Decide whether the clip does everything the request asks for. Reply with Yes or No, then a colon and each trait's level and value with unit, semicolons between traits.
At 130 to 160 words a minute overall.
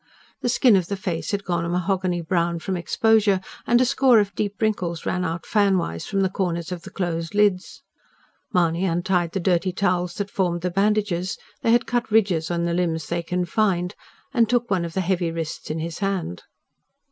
No: average, 200 wpm